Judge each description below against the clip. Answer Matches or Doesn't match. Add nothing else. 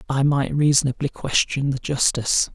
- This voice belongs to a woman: Doesn't match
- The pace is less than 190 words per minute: Matches